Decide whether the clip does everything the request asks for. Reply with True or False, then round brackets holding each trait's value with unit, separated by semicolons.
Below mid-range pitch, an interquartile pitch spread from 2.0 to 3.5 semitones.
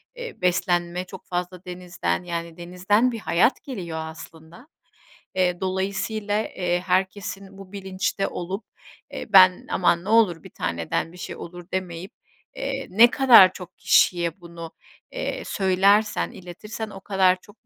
False (185 Hz; 2.5 semitones)